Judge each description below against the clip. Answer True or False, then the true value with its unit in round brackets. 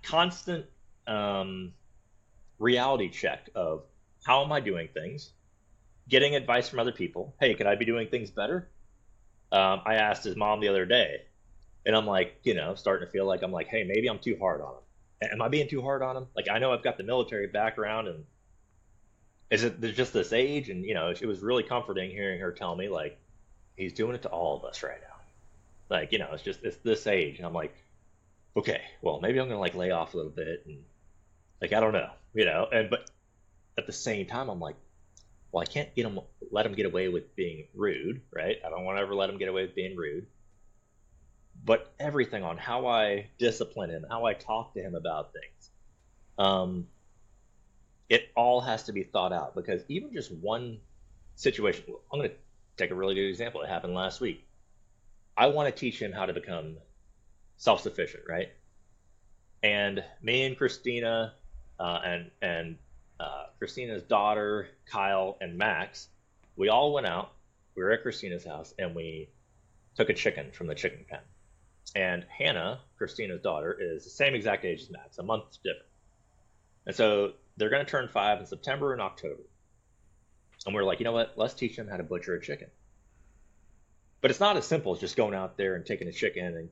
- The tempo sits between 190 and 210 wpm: True (195 wpm)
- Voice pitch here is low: True (100 Hz)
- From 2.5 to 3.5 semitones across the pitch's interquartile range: False (4.0 semitones)